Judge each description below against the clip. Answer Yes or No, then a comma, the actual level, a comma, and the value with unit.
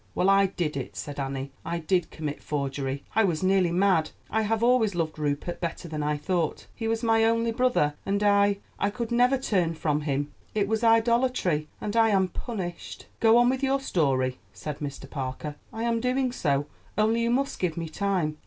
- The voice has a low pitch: No, high, 190 Hz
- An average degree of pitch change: No, wide, 6.9 semitones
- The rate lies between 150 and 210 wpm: Yes, average, 195 wpm